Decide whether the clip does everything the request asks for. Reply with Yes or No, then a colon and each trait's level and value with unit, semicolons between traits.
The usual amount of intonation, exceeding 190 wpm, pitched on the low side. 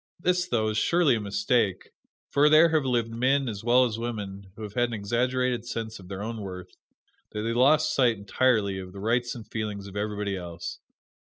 Yes: average, 4.0 semitones; fast, 205 wpm; low, 115 Hz